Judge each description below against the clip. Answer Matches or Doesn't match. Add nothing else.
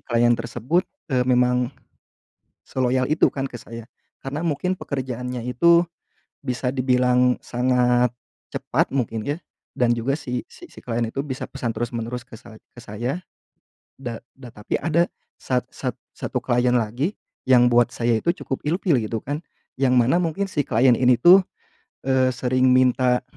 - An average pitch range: Doesn't match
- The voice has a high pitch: Doesn't match